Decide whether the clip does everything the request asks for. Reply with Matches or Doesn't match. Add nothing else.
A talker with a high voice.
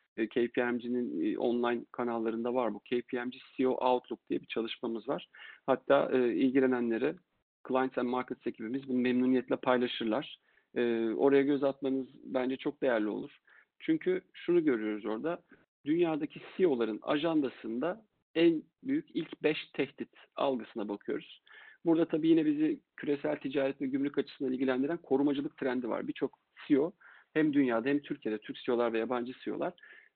Doesn't match